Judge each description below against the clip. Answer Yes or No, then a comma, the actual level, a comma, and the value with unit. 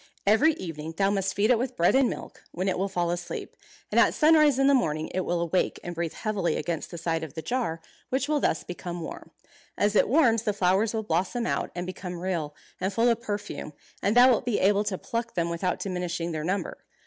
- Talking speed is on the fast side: Yes, fast, 230 wpm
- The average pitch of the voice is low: No, high, 190 Hz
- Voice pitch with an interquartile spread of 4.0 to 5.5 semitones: Yes, average, 5.0 semitones